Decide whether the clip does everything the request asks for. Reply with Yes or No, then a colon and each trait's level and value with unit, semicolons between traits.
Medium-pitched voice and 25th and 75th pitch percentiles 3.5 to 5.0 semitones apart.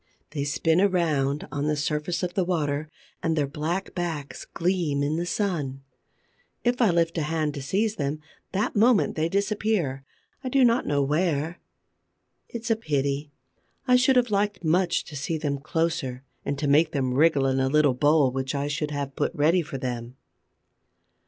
Yes: medium, 155 Hz; average, 4.2 semitones